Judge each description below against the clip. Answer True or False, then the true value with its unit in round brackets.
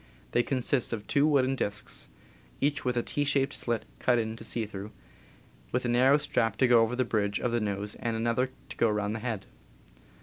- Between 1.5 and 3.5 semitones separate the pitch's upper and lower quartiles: True (2.8 semitones)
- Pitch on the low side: True (120 Hz)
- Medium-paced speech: False (215 wpm)